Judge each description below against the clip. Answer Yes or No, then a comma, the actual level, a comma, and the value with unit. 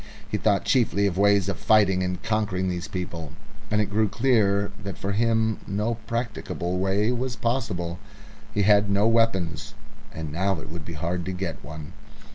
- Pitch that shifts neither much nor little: Yes, average, 3.3 semitones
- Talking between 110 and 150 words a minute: No, average, 175 wpm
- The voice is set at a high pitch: No, low, 100 Hz